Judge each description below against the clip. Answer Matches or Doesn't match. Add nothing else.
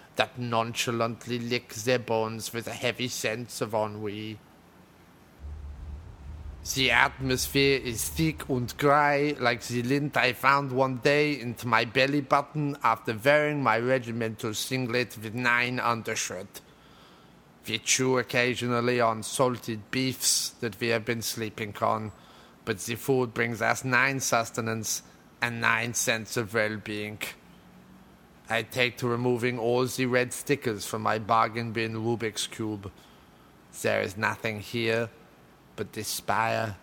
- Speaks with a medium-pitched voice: Doesn't match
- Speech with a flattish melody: Matches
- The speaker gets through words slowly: Matches